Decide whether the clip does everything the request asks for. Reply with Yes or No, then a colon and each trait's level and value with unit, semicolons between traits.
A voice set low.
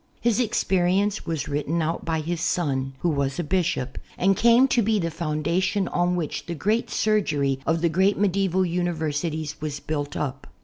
No: medium, 170 Hz